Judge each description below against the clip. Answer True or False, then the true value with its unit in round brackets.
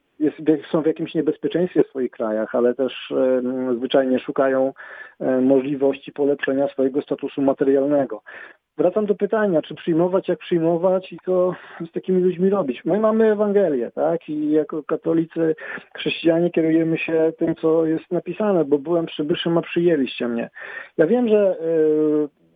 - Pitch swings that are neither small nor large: True (3.9 semitones)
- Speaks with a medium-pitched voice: True (160 Hz)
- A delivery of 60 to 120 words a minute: False (150 wpm)